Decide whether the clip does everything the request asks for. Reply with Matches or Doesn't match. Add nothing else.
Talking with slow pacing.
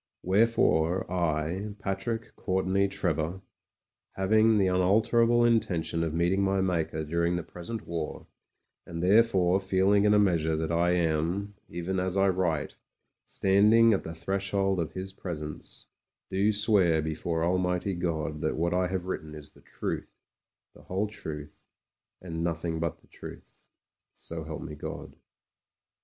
Doesn't match